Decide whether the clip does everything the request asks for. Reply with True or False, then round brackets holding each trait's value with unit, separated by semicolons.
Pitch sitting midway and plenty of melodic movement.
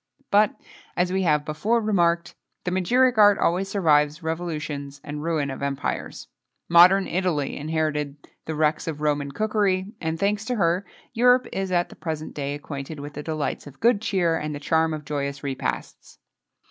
False (160 Hz; 4.5 semitones)